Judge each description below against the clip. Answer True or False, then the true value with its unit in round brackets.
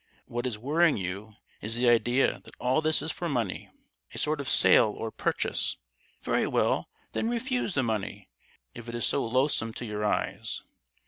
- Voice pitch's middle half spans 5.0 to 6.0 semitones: True (5.5 semitones)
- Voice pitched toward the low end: True (120 Hz)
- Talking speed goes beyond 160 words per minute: True (175 wpm)